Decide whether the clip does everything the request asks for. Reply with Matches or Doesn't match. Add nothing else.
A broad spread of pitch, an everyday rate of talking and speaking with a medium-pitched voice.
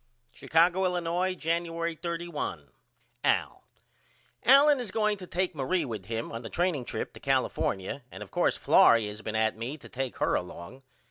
Matches